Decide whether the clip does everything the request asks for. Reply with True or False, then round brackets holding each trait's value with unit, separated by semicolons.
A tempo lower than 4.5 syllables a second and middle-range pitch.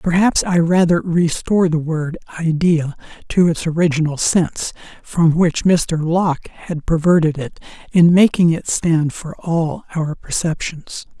True (4.2 syllables/s; 165 Hz)